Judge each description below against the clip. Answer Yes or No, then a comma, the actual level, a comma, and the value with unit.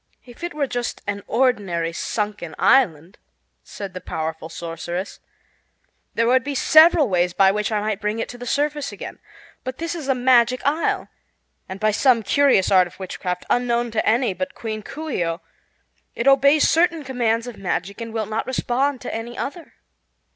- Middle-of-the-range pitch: No, high, 230 Hz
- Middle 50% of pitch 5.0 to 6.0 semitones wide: Yes, wide, 5.4 semitones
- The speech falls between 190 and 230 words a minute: No, average, 180 wpm